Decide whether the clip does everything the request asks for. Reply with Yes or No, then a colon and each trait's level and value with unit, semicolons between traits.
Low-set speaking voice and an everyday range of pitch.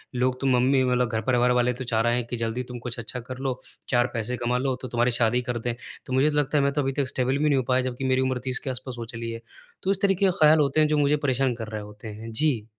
No: low, 125 Hz; narrow, 2.2 semitones